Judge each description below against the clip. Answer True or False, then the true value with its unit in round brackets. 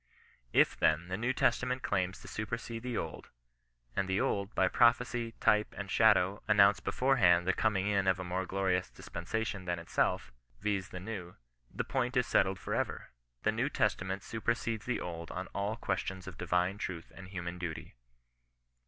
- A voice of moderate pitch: False (95 Hz)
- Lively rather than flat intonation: False (3.4 semitones)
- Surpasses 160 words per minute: True (180 wpm)